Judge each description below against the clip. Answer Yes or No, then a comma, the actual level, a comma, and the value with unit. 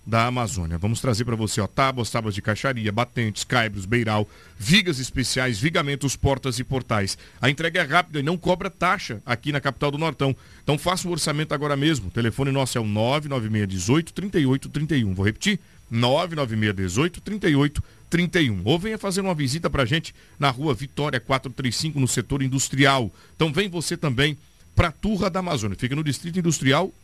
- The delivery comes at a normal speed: Yes, average, 170 wpm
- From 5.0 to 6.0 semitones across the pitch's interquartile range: Yes, wide, 5.5 semitones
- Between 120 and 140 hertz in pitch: Yes, low, 135 Hz